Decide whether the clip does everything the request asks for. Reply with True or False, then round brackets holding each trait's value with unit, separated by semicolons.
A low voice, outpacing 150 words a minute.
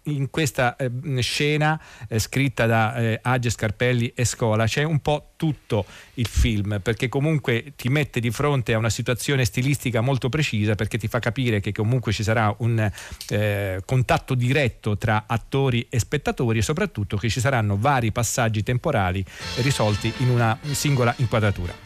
True (120 Hz; 165 wpm)